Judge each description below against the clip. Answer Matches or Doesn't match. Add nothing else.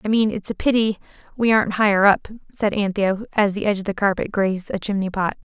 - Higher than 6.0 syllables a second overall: Matches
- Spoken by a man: Doesn't match